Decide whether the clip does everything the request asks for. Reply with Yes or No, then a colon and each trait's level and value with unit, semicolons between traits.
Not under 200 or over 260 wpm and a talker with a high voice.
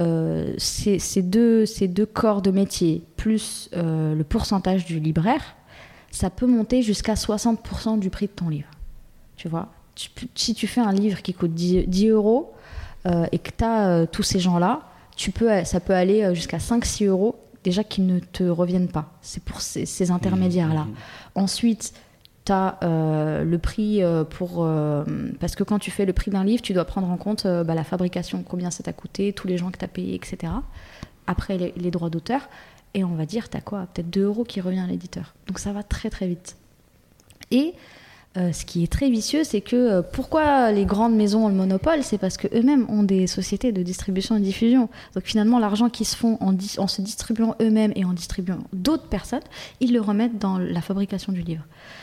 Yes: average, 210 wpm; high, 195 Hz